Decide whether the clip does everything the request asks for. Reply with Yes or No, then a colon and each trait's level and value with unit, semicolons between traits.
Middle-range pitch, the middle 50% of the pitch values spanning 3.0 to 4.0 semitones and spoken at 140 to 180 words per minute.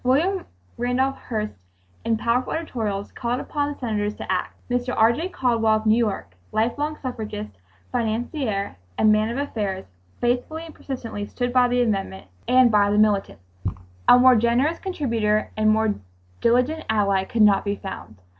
No: high, 230 Hz; average, 3.3 semitones; average, 165 wpm